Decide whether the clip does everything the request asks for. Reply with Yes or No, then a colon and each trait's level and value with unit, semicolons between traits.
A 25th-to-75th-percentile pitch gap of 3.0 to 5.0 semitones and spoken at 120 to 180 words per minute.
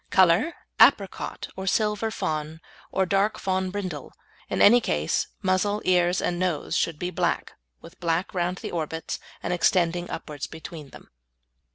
No: narrow, 2.6 semitones; average, 150 wpm